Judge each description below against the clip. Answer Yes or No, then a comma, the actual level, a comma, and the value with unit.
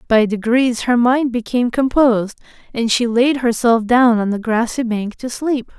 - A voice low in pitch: No, high, 240 Hz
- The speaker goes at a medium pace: Yes, average, 175 wpm